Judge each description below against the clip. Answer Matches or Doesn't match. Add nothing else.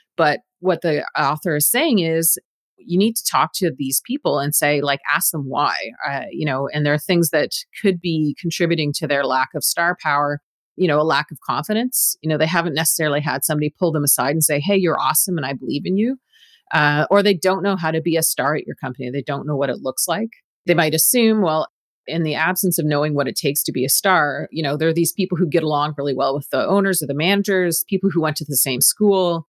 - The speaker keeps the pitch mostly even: Doesn't match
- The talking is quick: Matches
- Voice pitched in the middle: Matches